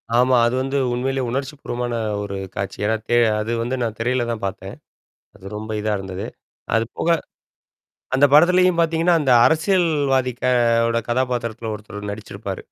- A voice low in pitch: Yes, low, 125 Hz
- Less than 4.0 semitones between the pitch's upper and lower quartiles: No, average, 4.3 semitones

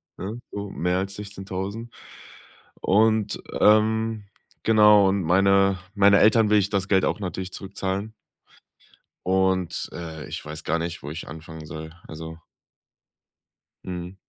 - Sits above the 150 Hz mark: No, very low, 95 Hz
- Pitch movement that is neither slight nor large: Yes, average, 3.1 semitones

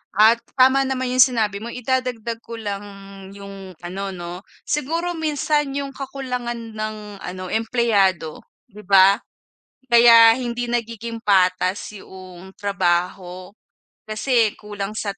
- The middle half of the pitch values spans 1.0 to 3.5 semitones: No, average, 3.9 semitones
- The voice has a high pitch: Yes, high, 220 Hz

